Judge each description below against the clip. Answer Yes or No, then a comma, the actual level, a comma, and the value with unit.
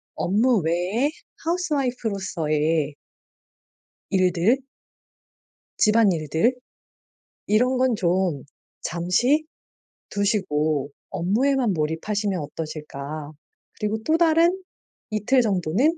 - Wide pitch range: Yes, wide, 7.6 semitones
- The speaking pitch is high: Yes, high, 200 Hz